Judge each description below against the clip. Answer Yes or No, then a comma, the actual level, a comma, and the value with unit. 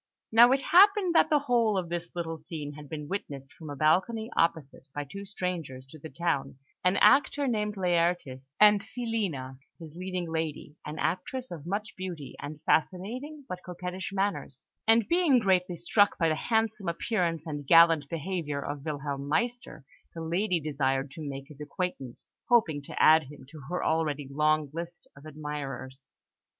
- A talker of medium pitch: Yes, medium, 165 Hz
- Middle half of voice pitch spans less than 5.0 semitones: No, wide, 5.4 semitones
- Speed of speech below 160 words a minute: No, average, 165 wpm